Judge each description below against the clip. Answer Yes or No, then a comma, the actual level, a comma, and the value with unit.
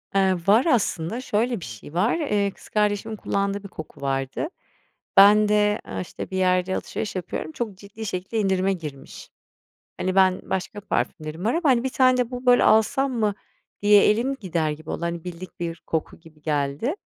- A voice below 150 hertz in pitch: No, high, 195 Hz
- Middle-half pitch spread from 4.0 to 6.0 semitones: Yes, average, 4.5 semitones